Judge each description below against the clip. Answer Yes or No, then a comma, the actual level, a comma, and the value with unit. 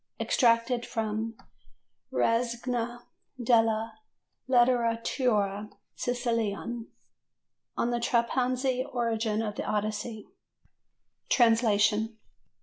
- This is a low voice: No, high, 230 Hz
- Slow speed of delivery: Yes, slow, 70 wpm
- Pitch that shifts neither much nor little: No, narrow, 1.7 semitones